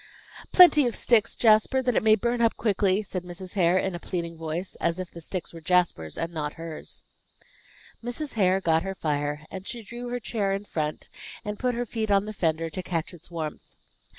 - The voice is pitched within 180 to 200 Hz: Yes, medium, 185 Hz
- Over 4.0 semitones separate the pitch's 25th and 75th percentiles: Yes, average, 4.7 semitones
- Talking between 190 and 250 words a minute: Yes, fast, 205 wpm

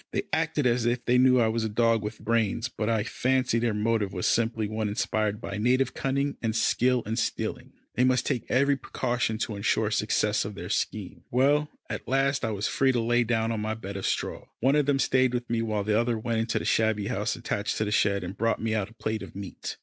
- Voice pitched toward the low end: Yes, low, 115 Hz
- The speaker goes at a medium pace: No, fast, 240 wpm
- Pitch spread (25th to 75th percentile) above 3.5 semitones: No, narrow, 2.6 semitones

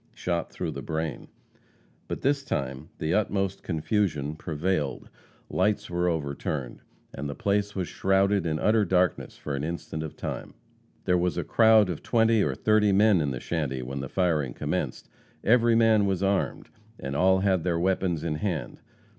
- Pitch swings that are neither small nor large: Yes, average, 4.8 semitones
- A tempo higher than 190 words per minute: No, average, 170 wpm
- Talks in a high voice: No, very low, 90 Hz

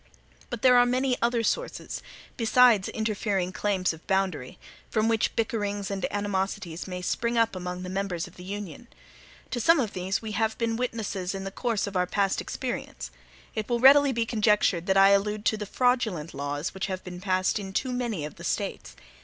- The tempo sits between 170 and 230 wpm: Yes, average, 195 wpm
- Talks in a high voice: Yes, high, 205 Hz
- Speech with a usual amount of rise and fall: Yes, average, 3.6 semitones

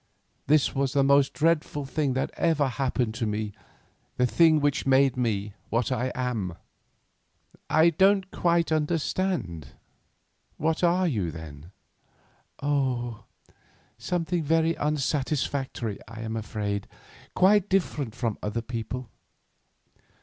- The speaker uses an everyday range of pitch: No, wide, 5.9 semitones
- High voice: No, low, 135 Hz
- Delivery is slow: Yes, slow, 115 wpm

